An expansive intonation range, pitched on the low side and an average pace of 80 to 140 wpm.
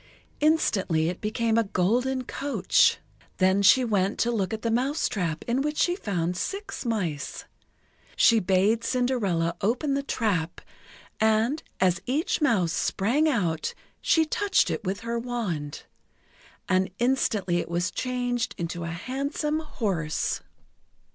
No: wide, 5.9 semitones; high, 220 Hz; slow, 135 wpm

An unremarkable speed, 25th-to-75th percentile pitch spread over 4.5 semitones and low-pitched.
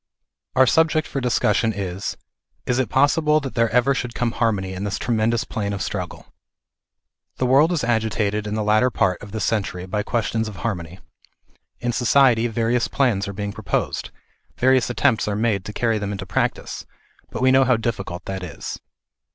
No: average, 180 wpm; average, 3.4 semitones; low, 110 Hz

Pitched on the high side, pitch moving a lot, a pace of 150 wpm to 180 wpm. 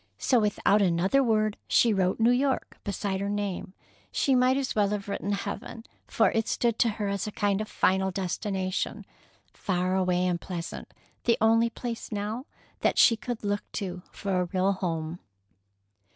No: high, 205 Hz; average, 3.2 semitones; average, 170 wpm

